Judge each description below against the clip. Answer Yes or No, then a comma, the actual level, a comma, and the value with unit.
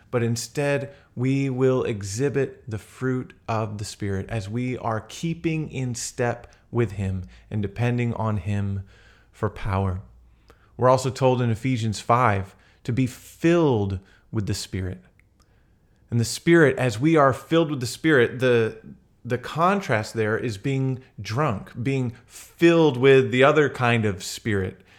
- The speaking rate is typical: Yes, average, 145 wpm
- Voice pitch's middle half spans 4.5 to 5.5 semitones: No, average, 4.1 semitones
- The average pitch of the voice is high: No, low, 120 Hz